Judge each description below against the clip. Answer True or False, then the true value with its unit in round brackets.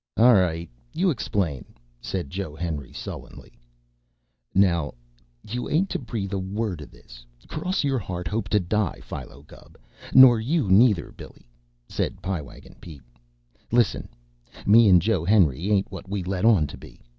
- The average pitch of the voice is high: False (95 Hz)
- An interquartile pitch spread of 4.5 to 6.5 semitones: True (5.0 semitones)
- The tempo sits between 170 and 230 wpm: False (155 wpm)